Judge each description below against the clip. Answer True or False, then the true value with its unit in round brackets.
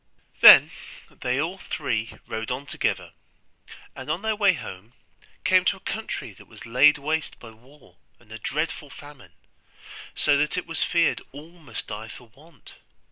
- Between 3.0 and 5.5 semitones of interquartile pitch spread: True (5.1 semitones)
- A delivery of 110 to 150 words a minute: False (165 wpm)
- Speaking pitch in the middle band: True (145 Hz)